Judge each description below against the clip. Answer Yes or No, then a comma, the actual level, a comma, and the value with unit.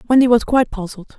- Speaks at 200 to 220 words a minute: Yes, fast, 205 wpm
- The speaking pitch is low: No, high, 230 Hz